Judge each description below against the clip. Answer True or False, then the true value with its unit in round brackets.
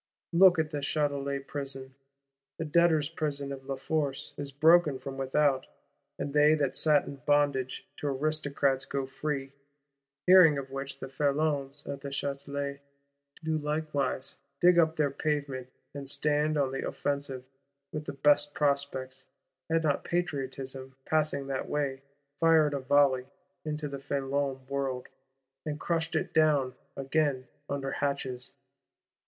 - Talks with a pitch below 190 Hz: True (140 Hz)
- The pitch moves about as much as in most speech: False (1.9 semitones)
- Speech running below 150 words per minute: True (140 wpm)